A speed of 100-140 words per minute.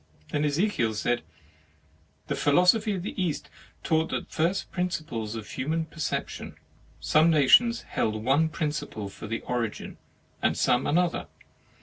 Yes: slow, 135 wpm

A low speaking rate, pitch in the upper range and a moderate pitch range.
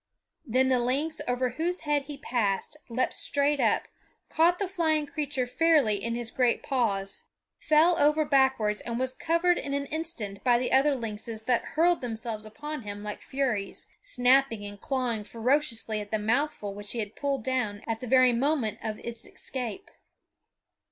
No: average, 170 wpm; very high, 255 Hz; average, 4.9 semitones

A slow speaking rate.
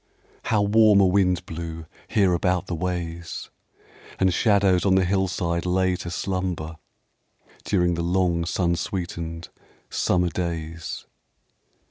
Yes: slow, 120 wpm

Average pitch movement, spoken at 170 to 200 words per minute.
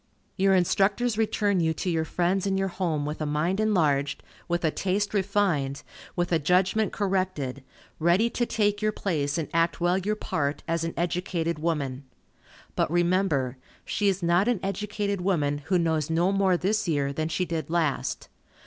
Yes: average, 3.7 semitones; average, 175 wpm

